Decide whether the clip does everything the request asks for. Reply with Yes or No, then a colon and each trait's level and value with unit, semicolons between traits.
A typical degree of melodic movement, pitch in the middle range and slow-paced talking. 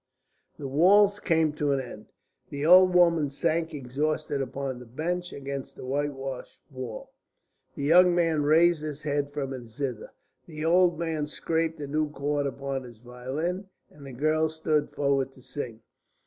No: average, 3.1 semitones; medium, 145 Hz; average, 160 wpm